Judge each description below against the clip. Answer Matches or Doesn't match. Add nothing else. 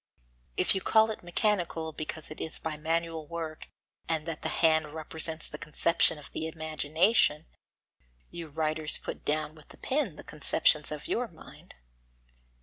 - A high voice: Doesn't match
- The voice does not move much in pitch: Matches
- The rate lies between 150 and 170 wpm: Matches